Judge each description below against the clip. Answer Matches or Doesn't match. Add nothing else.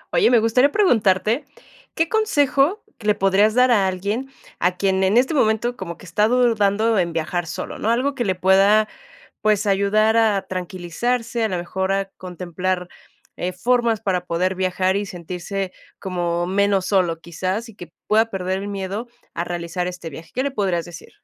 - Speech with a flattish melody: Doesn't match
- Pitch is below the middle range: Doesn't match